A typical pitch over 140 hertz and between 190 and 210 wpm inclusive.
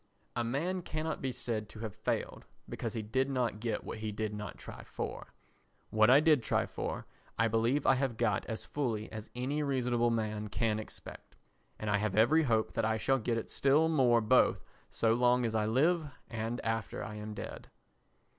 No: low, 115 Hz; average, 195 wpm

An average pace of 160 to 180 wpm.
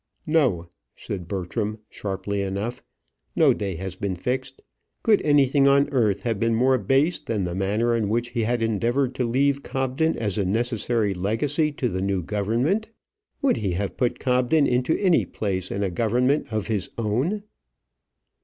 Yes: average, 165 wpm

